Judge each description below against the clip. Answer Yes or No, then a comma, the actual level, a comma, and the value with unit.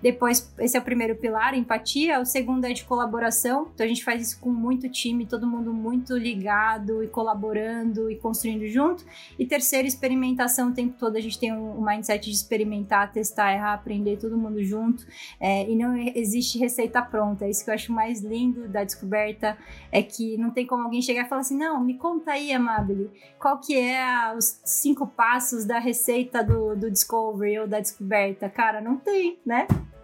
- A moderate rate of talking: No, fast, 195 wpm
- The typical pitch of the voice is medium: No, high, 230 Hz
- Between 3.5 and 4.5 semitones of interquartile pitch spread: No, narrow, 2.4 semitones